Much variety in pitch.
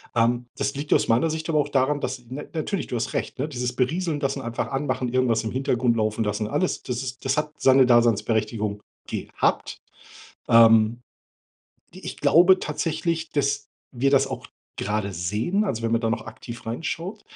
No: average, 4.2 semitones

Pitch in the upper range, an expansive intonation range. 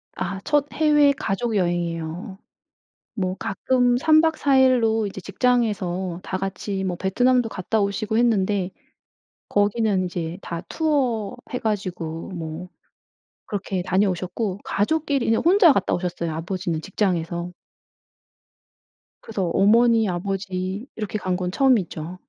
No: high, 195 Hz; average, 4.5 semitones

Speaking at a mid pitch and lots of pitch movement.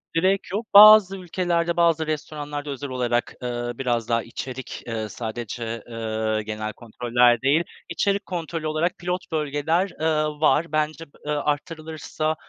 Yes: medium, 150 Hz; wide, 5.7 semitones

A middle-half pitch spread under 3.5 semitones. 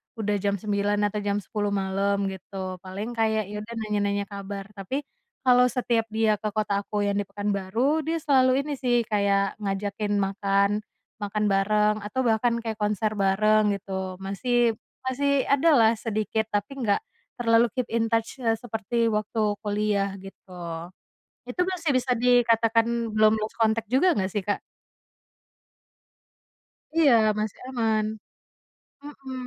Yes: average, 2.7 semitones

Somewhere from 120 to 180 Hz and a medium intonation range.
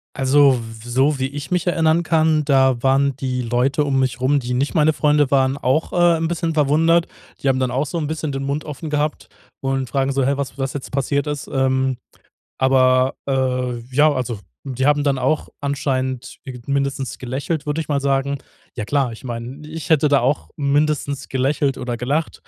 No: medium, 140 Hz; narrow, 2.2 semitones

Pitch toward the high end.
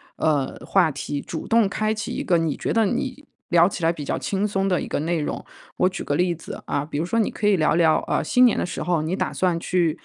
No: medium, 175 Hz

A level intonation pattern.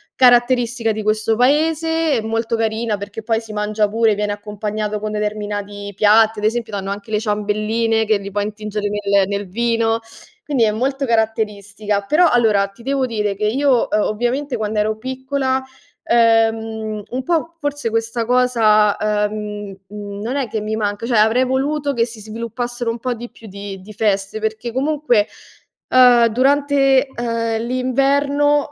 No: average, 3.0 semitones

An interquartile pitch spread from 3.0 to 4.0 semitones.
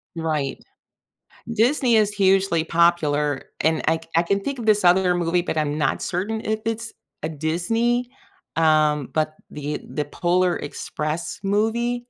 No: wide, 5.6 semitones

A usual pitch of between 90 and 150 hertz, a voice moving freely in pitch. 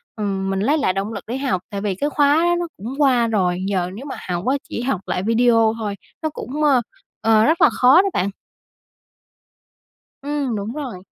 No: high, 230 Hz; wide, 6.1 semitones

